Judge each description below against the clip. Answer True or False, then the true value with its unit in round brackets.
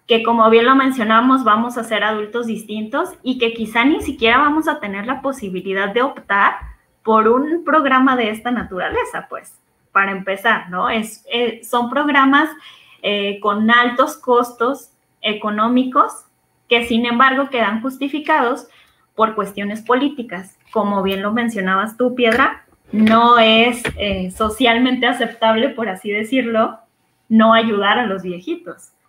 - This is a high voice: True (230 Hz)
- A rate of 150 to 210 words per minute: False (140 wpm)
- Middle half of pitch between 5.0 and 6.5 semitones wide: False (3.6 semitones)